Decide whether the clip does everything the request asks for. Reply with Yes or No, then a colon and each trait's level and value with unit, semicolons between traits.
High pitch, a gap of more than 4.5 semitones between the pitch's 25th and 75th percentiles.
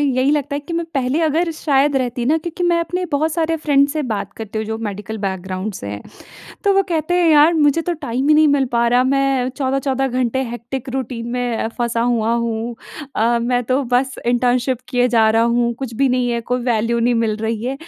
No: very high, 250 Hz; average, 3.4 semitones